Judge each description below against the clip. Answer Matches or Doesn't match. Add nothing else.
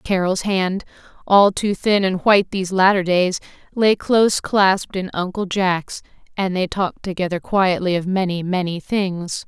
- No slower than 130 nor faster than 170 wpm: Matches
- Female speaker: Matches